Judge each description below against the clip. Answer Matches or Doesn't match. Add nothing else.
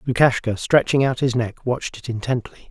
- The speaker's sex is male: Matches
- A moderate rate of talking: Matches